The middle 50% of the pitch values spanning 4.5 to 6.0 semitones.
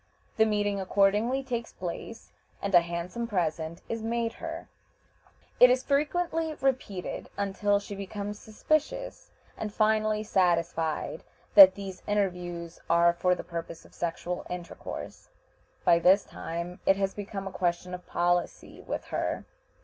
No: average, 3.9 semitones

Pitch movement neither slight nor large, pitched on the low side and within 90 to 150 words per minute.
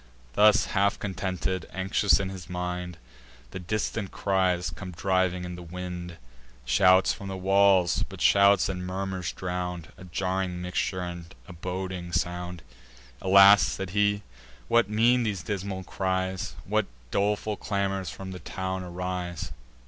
No: narrow, 1.6 semitones; very low, 95 Hz; average, 140 wpm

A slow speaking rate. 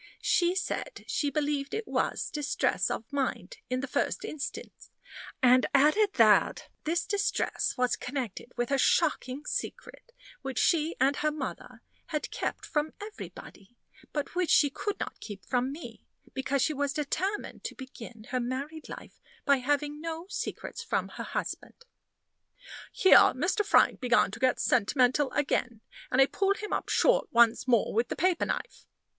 No: average, 160 wpm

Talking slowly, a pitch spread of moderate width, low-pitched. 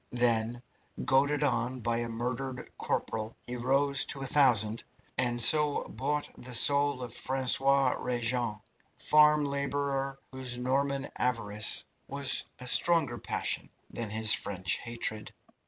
Yes: slow, 125 wpm; average, 3.0 semitones; low, 125 Hz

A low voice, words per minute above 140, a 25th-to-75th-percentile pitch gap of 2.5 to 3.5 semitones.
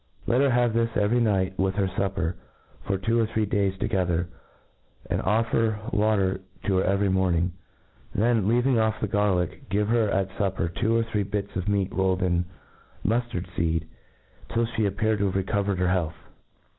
Yes: low, 100 Hz; average, 180 wpm; average, 2.9 semitones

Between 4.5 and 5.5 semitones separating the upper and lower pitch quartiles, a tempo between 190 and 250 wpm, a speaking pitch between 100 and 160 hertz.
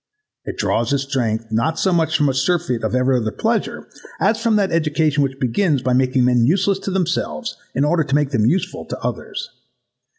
Yes: average, 5.1 semitones; average, 200 wpm; medium, 140 Hz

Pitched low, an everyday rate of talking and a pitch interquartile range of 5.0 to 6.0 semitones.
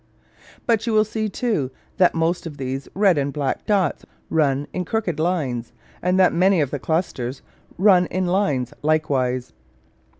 No: medium, 165 Hz; average, 160 wpm; wide, 5.4 semitones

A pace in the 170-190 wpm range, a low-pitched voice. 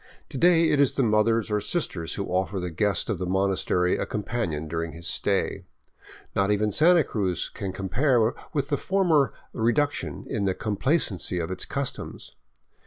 Yes: average, 180 wpm; low, 105 Hz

